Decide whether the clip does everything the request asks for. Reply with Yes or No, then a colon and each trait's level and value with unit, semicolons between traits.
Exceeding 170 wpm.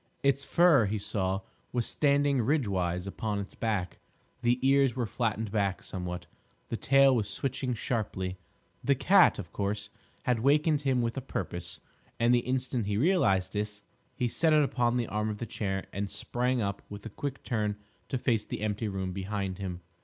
Yes: average, 180 wpm